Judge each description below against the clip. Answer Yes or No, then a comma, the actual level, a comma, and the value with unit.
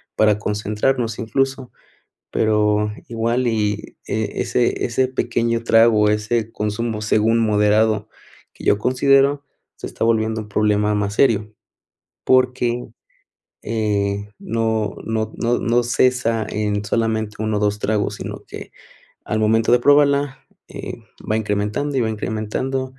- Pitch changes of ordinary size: No, narrow, 2.3 semitones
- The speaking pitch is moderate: No, low, 110 Hz